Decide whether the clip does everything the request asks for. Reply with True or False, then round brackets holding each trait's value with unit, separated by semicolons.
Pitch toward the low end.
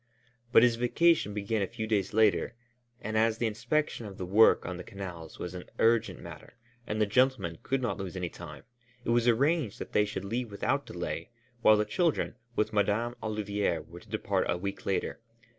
True (105 Hz)